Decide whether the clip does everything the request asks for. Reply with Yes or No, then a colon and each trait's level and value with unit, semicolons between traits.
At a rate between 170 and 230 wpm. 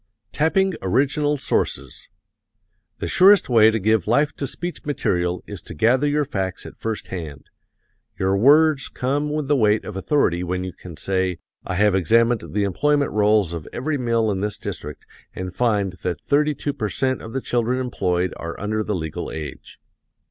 Yes: average, 175 wpm